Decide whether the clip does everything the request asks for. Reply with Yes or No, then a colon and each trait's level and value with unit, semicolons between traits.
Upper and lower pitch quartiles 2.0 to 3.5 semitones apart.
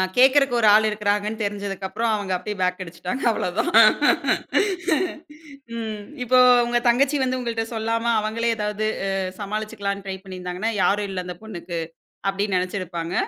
Yes: average, 3.1 semitones